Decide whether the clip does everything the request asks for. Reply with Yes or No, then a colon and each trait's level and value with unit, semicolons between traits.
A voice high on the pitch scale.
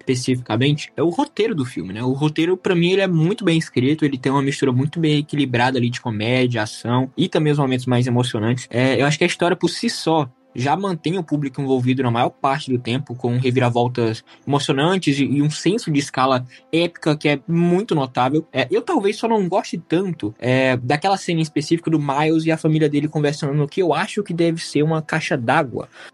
No: medium, 145 Hz